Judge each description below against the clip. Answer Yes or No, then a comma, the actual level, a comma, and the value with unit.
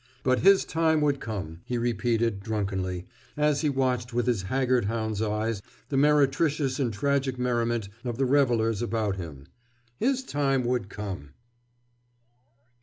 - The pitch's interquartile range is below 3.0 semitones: No, average, 4.1 semitones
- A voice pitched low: Yes, low, 120 Hz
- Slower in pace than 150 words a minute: Yes, slow, 135 wpm